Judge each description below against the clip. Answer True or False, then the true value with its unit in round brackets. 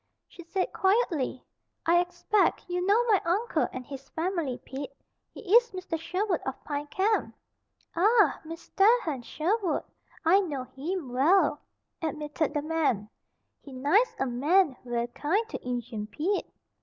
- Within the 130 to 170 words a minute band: True (145 wpm)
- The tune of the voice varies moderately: False (6.0 semitones)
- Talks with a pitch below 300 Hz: False (330 Hz)